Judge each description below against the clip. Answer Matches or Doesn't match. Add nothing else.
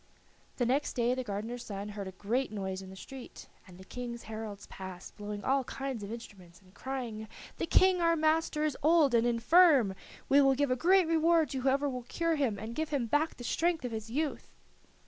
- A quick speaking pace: Matches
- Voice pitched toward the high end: Matches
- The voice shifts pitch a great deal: Matches